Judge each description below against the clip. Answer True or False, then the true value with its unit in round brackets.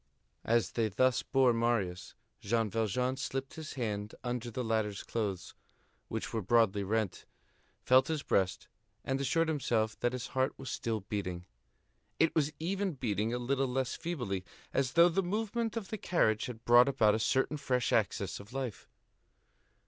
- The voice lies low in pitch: True (120 Hz)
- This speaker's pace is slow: False (165 wpm)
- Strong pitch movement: False (4.0 semitones)